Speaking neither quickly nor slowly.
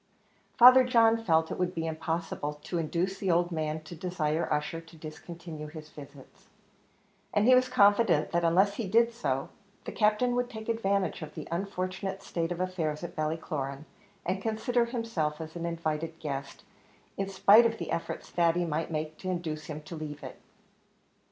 Yes: average, 175 wpm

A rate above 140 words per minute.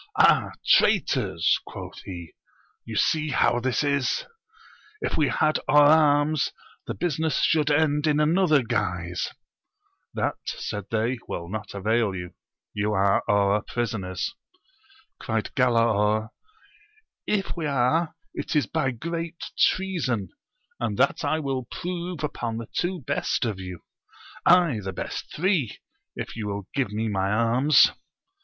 No: slow, 135 wpm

